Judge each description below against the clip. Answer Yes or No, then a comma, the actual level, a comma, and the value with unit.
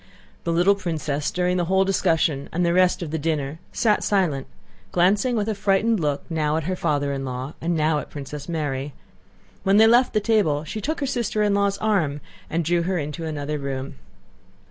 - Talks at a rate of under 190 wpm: No, average, 200 wpm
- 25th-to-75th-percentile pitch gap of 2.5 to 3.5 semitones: No, average, 5.1 semitones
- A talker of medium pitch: Yes, medium, 170 Hz